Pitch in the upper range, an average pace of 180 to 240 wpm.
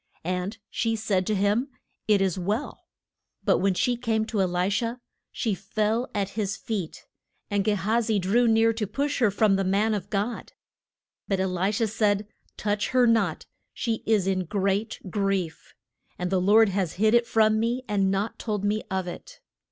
Yes: high, 210 Hz; average, 190 wpm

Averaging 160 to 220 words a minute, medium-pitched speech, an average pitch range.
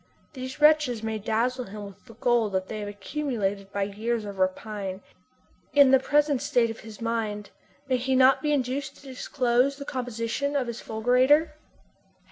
No: average, 170 wpm; high, 240 Hz; average, 4.0 semitones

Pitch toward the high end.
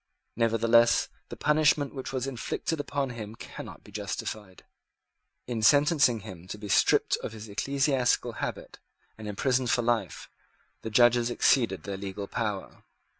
No: low, 115 Hz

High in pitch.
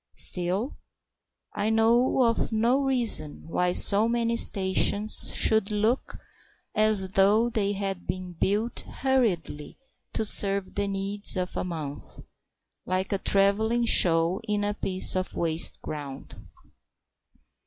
Yes: high, 200 Hz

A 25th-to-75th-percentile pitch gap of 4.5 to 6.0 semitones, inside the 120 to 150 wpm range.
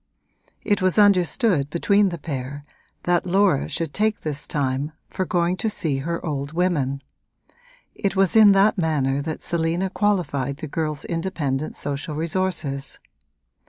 Yes: average, 4.8 semitones; average, 140 wpm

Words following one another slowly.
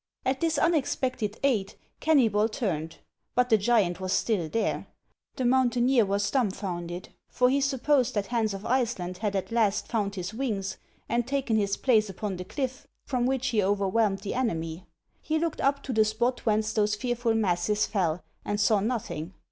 No: average, 170 wpm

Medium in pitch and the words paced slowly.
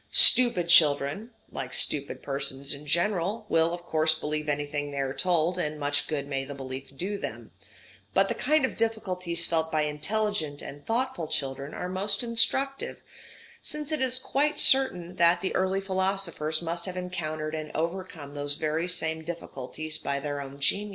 No: medium, 165 Hz; average, 170 wpm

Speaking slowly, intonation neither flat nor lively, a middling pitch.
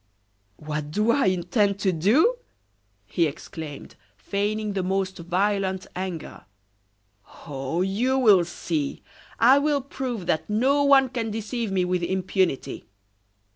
No: slow, 125 wpm; average, 4.7 semitones; high, 195 Hz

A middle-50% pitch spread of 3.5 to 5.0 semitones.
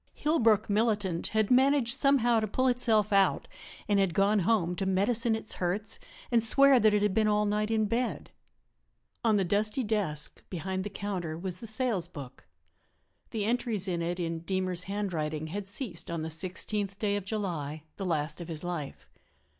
Yes: average, 3.8 semitones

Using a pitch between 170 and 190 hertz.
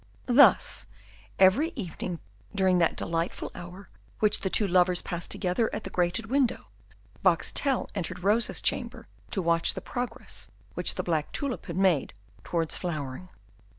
Yes: medium, 185 Hz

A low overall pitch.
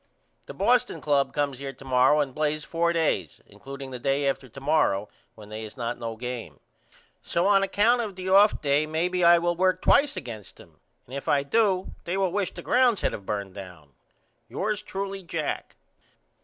No: medium, 150 Hz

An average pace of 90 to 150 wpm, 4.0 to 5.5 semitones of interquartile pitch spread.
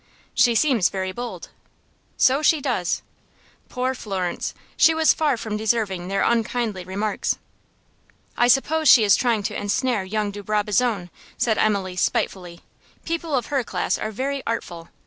Yes: average, 145 wpm; average, 4.7 semitones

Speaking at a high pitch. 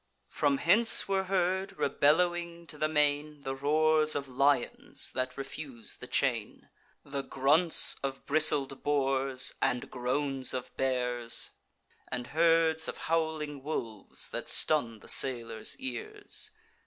No: medium, 145 Hz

